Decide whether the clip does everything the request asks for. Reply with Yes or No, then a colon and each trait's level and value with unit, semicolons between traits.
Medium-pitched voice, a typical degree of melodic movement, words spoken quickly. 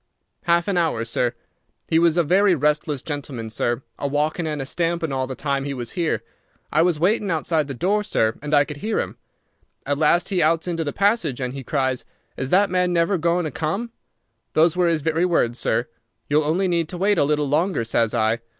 Yes: medium, 155 Hz; average, 4.0 semitones; fast, 215 wpm